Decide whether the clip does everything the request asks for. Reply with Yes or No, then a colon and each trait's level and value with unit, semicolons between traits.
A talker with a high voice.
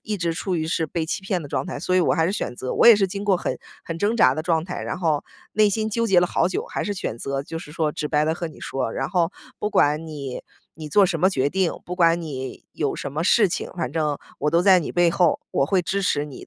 No: medium, 170 Hz